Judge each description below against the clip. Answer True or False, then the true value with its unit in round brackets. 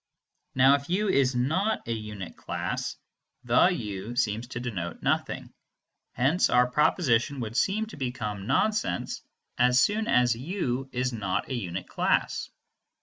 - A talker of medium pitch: False (125 Hz)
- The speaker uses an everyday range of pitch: True (4.4 semitones)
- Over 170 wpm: False (145 wpm)